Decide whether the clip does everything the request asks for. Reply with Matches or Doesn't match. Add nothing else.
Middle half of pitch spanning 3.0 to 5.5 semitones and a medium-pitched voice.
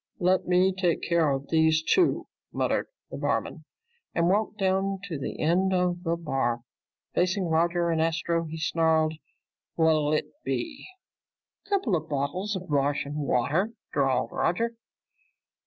Matches